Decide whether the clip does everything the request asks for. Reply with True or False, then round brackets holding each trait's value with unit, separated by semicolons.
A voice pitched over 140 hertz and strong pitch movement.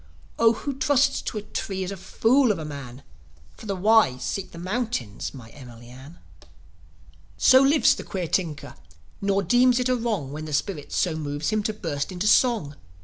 True (190 Hz; 7.7 semitones)